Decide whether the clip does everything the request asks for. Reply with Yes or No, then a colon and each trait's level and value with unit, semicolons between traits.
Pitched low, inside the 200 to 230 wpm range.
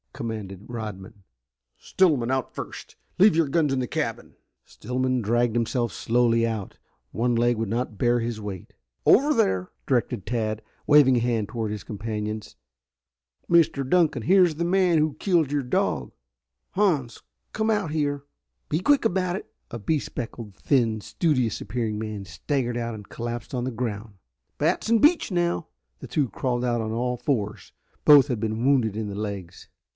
No: low, 120 Hz; average, 165 wpm